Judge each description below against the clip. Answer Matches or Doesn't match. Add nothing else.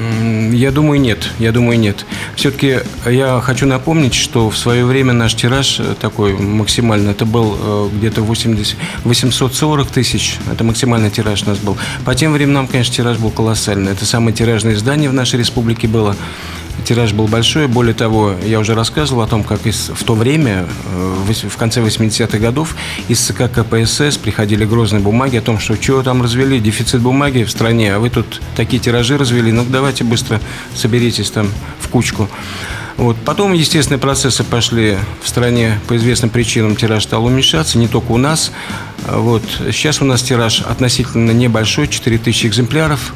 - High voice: Doesn't match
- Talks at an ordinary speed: Doesn't match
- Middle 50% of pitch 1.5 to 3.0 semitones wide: Matches